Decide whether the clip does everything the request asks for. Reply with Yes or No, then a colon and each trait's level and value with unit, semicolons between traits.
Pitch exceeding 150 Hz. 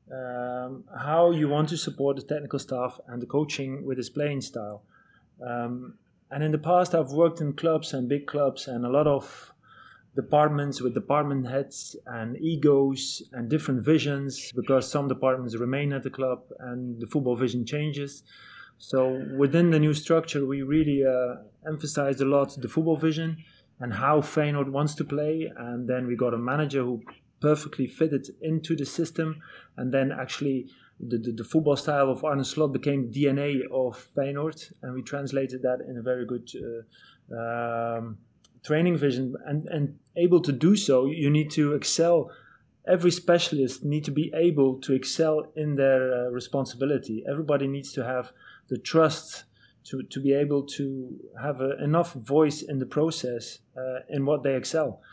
No: medium, 140 Hz